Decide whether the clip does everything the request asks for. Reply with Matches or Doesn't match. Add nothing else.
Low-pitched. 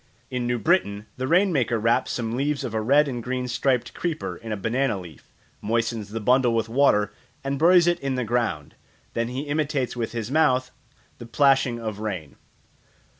Matches